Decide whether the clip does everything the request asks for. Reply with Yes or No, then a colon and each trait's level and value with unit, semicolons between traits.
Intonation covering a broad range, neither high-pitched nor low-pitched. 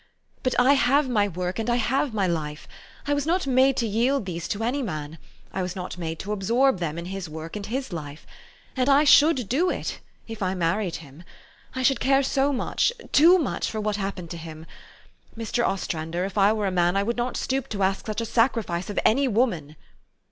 No: wide, 6.5 semitones; high, 210 Hz